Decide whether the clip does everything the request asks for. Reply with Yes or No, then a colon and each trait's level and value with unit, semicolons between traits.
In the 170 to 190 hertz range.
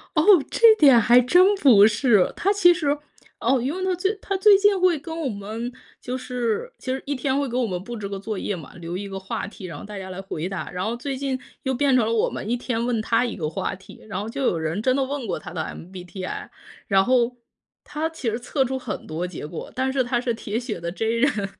No: high, 240 Hz